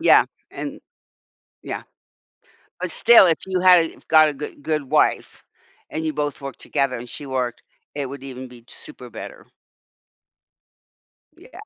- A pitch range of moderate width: Yes, average, 3.5 semitones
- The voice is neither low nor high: Yes, medium, 145 Hz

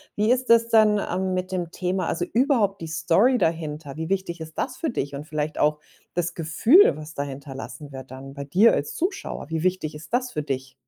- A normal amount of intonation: No, wide, 5.7 semitones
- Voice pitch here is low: No, medium, 170 Hz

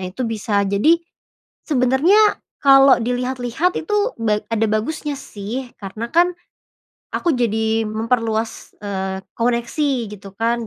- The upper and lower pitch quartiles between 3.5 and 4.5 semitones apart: Yes, average, 3.9 semitones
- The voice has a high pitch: Yes, high, 235 Hz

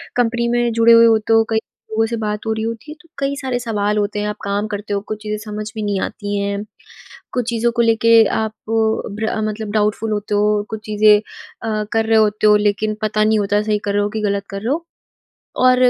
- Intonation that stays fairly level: Yes, narrow, 1.5 semitones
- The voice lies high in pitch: Yes, high, 215 Hz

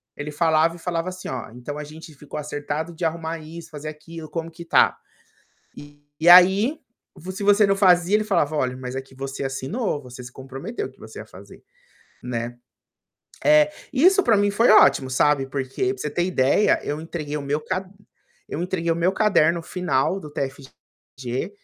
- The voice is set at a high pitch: No, medium, 160 Hz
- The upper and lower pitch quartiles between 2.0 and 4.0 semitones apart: No, average, 4.8 semitones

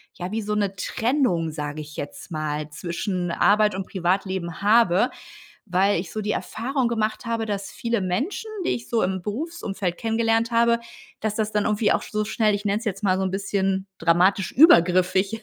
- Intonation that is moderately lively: Yes, average, 3.5 semitones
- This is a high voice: Yes, high, 200 Hz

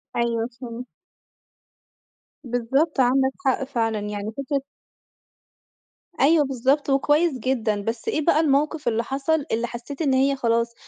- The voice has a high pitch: Yes, very high, 260 Hz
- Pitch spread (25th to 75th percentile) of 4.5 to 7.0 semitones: No, average, 3.3 semitones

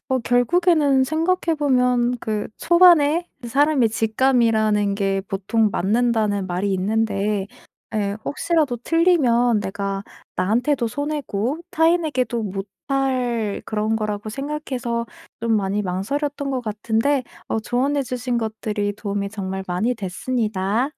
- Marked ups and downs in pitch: No, average, 4.9 semitones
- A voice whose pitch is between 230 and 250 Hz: Yes, high, 235 Hz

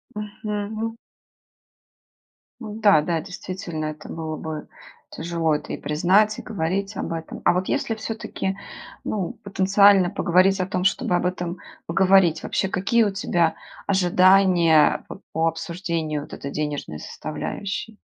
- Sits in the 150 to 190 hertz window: Yes, medium, 185 Hz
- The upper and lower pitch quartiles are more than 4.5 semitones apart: No, average, 3.4 semitones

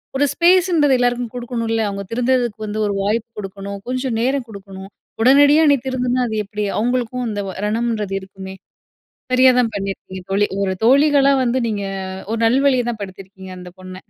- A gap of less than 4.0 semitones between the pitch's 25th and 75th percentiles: No, average, 4.3 semitones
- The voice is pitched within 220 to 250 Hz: Yes, high, 230 Hz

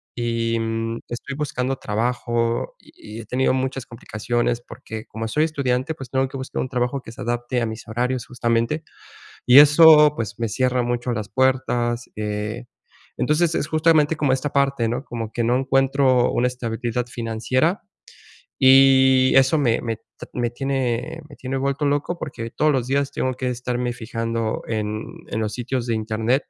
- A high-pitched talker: No, low, 125 Hz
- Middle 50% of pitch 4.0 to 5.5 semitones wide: No, narrow, 2.6 semitones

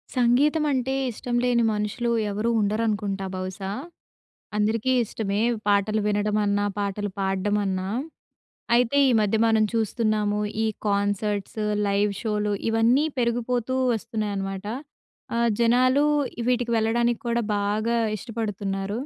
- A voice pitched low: No, high, 215 Hz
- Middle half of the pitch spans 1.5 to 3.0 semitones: Yes, narrow, 2.6 semitones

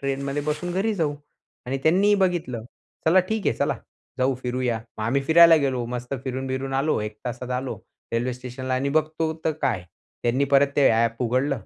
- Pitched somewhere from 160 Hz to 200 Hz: No, low, 135 Hz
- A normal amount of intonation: Yes, average, 4.0 semitones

